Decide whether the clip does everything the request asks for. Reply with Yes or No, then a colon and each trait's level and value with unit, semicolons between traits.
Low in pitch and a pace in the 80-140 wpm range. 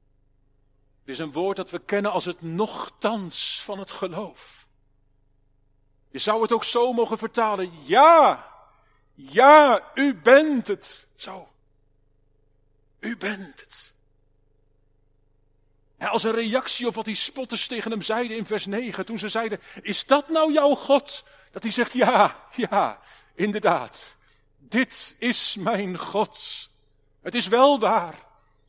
No: high, 200 Hz; slow, 135 wpm